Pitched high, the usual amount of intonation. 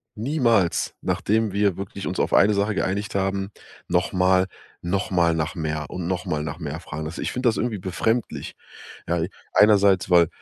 No: very low, 95 Hz; average, 3.1 semitones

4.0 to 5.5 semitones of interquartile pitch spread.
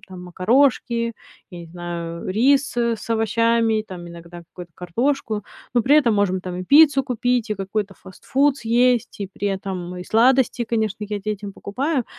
Yes: average, 4.7 semitones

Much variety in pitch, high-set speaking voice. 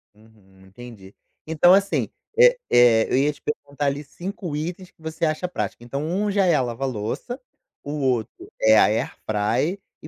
No: wide, 7.4 semitones; medium, 140 Hz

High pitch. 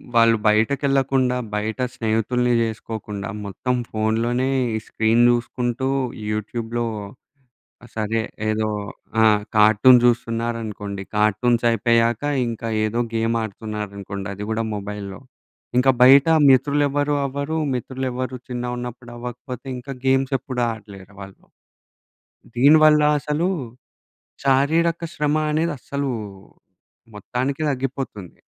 No: low, 120 Hz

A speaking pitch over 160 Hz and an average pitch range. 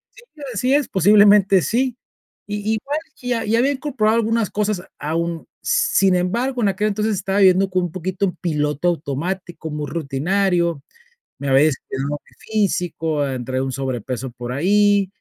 No: medium, 185 Hz; wide, 5.9 semitones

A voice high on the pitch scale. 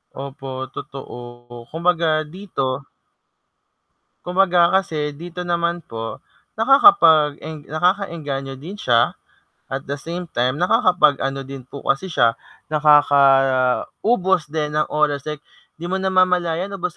No: medium, 150 Hz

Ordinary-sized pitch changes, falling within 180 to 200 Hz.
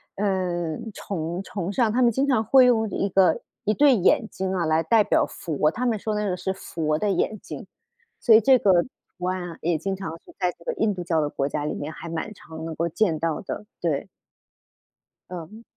Yes: average, 4.6 semitones; medium, 185 Hz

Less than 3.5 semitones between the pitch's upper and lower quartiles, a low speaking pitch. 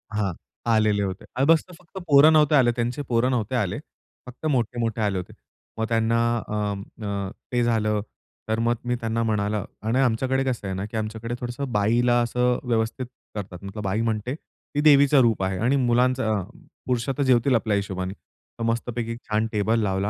Yes: average, 2.9 semitones; low, 115 Hz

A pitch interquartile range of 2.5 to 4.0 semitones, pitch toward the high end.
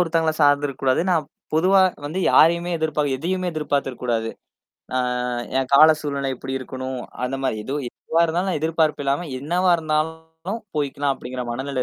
No: average, 3.4 semitones; medium, 150 Hz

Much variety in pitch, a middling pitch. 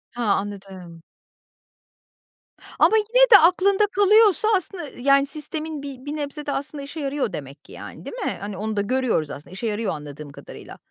No: wide, 8.2 semitones; very high, 275 Hz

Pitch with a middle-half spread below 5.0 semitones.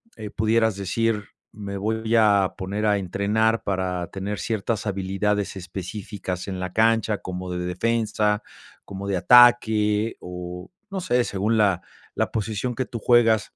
Yes: average, 2.8 semitones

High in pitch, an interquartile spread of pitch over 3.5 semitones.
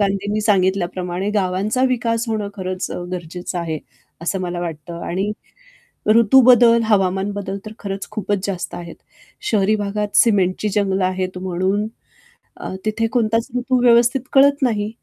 No: high, 200 Hz; average, 3.0 semitones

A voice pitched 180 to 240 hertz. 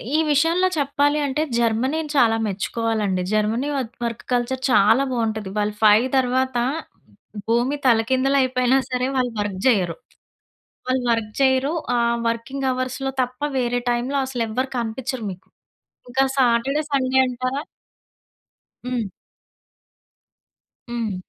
No: very high, 250 Hz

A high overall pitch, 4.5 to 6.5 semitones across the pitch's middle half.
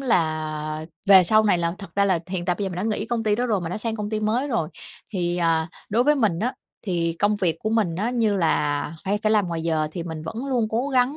Yes: high, 200 Hz; average, 4.8 semitones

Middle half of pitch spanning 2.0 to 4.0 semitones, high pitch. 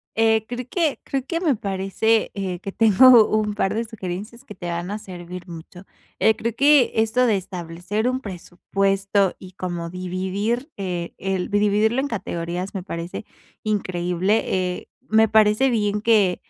Yes: average, 3.5 semitones; high, 200 Hz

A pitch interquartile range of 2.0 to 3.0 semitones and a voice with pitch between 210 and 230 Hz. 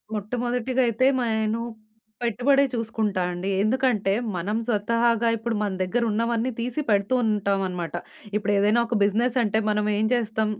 Yes: narrow, 2.5 semitones; high, 220 Hz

